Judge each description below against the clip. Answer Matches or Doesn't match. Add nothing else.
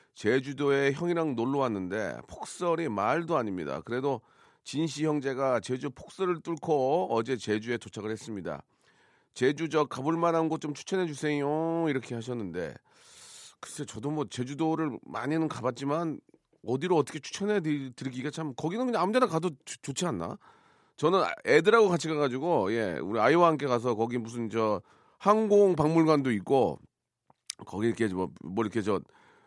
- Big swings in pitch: Doesn't match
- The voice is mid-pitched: Matches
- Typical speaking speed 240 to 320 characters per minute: Doesn't match